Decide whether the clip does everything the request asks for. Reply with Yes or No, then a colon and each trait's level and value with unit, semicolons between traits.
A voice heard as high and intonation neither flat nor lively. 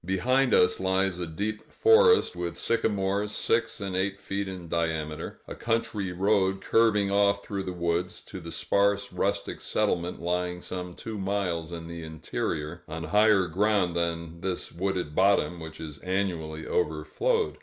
No: very low, 95 Hz; average, 3.1 semitones